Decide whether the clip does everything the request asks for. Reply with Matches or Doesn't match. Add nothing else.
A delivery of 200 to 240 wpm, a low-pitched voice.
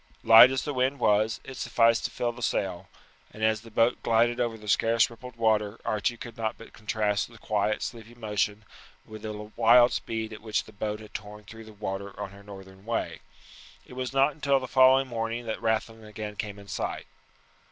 Matches